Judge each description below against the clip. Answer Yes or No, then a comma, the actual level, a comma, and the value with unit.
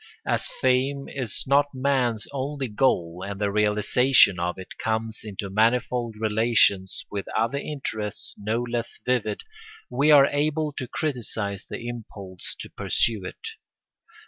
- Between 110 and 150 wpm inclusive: Yes, slow, 135 wpm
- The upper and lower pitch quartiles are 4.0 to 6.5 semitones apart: Yes, average, 4.4 semitones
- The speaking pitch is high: No, low, 115 Hz